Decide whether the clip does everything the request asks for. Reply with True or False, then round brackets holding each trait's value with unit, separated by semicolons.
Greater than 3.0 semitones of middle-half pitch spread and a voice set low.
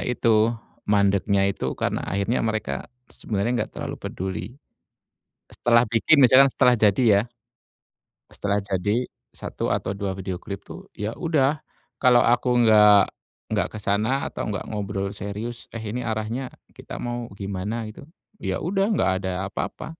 True (3.4 semitones; 110 Hz)